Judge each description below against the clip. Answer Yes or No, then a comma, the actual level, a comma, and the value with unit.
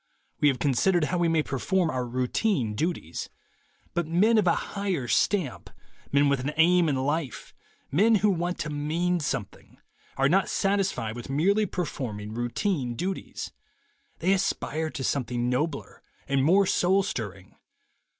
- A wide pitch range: Yes, wide, 5.9 semitones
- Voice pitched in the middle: Yes, medium, 155 Hz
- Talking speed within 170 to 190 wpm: No, average, 150 wpm